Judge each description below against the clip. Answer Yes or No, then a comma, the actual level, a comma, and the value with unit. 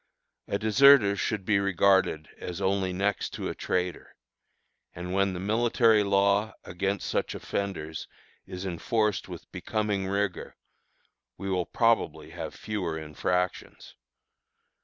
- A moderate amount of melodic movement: No, narrow, 2.3 semitones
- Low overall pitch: Yes, low, 100 Hz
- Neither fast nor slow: No, slow, 120 wpm